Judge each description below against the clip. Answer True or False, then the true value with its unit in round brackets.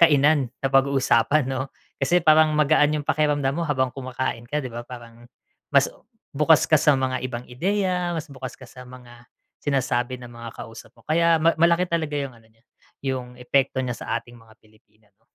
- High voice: False (135 Hz)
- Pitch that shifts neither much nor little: True (3.9 semitones)